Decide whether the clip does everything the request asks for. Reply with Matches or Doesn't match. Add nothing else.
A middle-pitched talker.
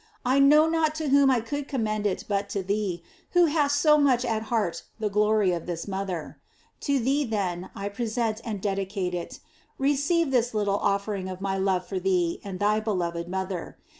Doesn't match